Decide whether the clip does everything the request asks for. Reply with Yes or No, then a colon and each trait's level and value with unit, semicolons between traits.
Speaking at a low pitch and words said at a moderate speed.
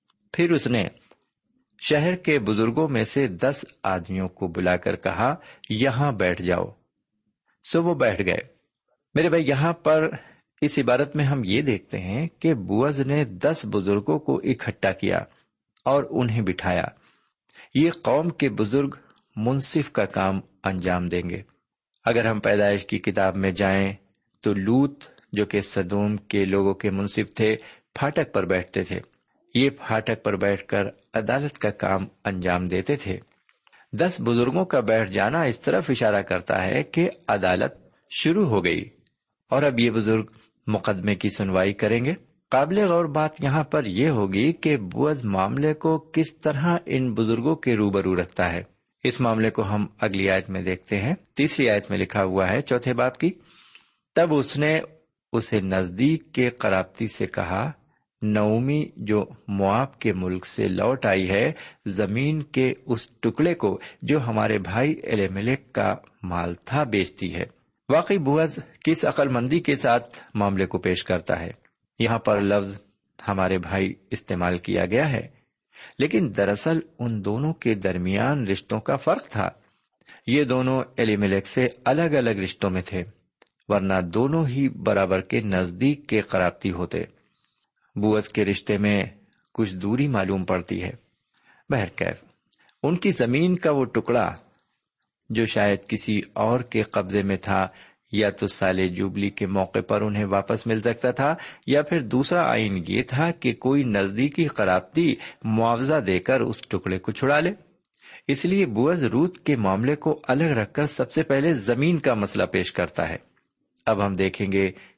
Yes: low, 110 Hz; average, 160 wpm